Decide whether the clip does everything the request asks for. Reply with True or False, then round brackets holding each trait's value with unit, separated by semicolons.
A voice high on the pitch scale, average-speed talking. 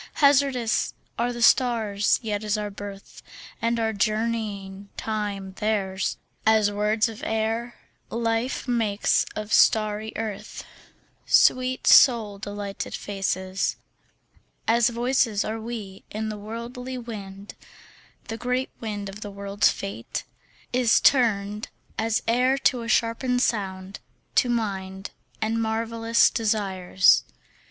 False (220 Hz; 115 wpm)